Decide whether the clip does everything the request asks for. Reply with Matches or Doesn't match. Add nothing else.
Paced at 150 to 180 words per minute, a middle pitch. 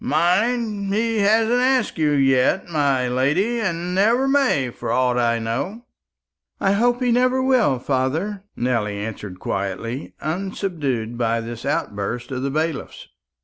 Doesn't match